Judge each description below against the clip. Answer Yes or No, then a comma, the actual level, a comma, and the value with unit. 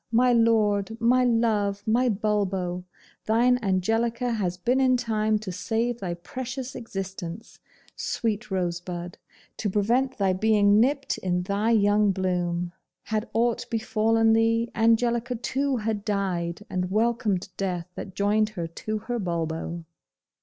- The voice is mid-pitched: No, high, 215 Hz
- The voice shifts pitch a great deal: No, average, 3.6 semitones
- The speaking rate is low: Yes, slow, 130 wpm